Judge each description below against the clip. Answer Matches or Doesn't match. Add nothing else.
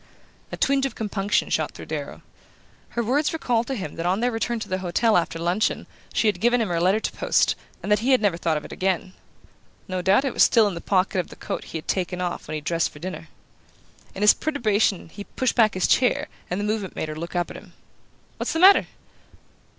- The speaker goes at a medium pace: Doesn't match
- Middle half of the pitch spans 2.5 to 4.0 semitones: Doesn't match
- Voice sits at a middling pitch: Doesn't match